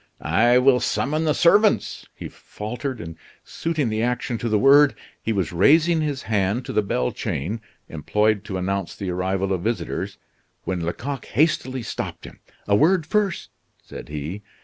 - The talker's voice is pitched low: Yes, low, 115 Hz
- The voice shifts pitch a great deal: Yes, wide, 7.0 semitones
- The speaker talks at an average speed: Yes, average, 165 wpm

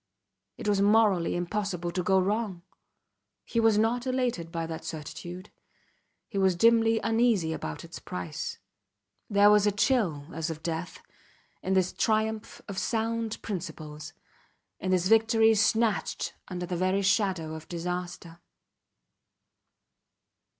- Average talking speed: No, slow, 130 wpm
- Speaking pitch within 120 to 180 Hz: No, high, 190 Hz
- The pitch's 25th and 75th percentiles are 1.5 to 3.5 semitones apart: No, average, 4.3 semitones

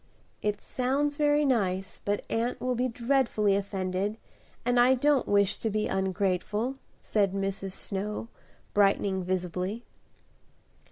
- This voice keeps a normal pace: No, slow, 120 wpm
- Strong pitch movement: No, average, 4.3 semitones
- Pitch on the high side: Yes, high, 210 Hz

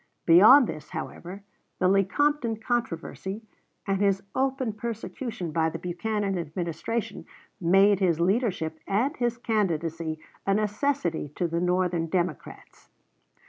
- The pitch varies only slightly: No, average, 4.8 semitones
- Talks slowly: Yes, slow, 115 wpm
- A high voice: Yes, high, 195 Hz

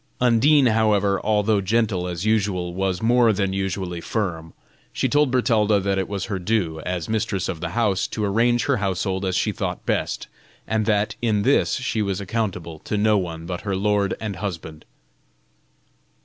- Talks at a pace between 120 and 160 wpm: No, average, 175 wpm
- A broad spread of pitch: No, average, 3.1 semitones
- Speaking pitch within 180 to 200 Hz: No, low, 100 Hz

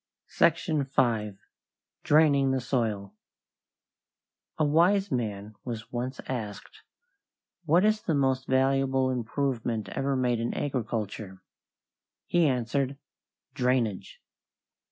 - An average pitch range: Yes, average, 3.5 semitones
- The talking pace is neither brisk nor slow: No, slow, 95 wpm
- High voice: No, low, 130 Hz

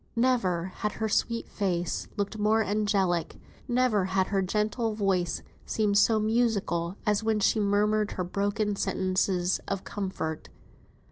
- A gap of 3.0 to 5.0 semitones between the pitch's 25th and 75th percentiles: No, narrow, 2.5 semitones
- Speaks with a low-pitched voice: No, high, 205 Hz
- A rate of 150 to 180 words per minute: No, slow, 135 wpm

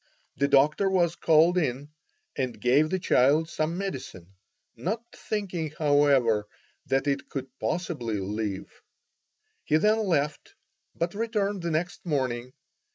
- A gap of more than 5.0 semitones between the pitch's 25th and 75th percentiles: Yes, wide, 5.4 semitones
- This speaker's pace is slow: Yes, slow, 125 wpm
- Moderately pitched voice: Yes, medium, 150 Hz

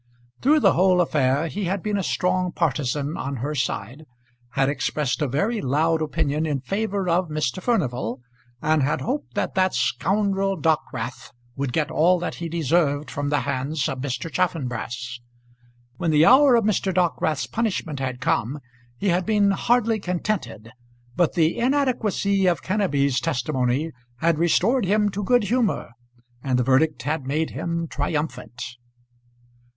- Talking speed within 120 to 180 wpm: Yes, average, 155 wpm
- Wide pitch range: Yes, wide, 5.7 semitones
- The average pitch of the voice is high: No, medium, 160 Hz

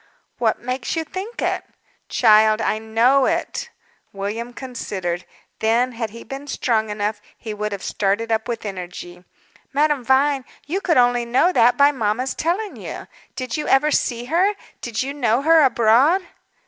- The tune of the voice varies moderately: Yes, average, 4.6 semitones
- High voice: Yes, high, 245 Hz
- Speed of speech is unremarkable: Yes, average, 160 wpm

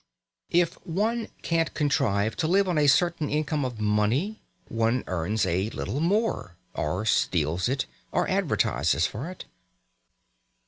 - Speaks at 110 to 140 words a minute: Yes, slow, 135 wpm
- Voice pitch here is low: Yes, low, 130 Hz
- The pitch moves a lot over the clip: Yes, wide, 8.5 semitones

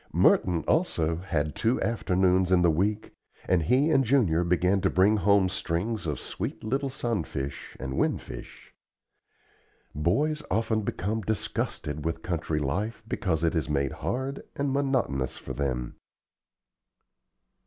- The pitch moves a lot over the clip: Yes, wide, 5.8 semitones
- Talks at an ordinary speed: No, slow, 130 wpm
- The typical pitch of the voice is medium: No, very low, 95 Hz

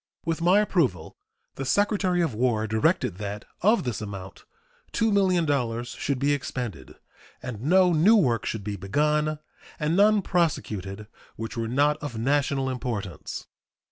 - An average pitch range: No, wide, 7.5 semitones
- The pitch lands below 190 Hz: Yes, low, 135 Hz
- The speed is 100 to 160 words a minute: Yes, average, 140 wpm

